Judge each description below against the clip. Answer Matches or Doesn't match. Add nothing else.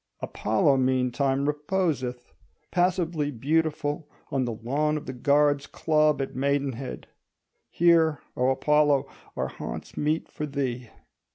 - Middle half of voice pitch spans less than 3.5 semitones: Matches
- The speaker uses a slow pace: Matches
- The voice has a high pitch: Doesn't match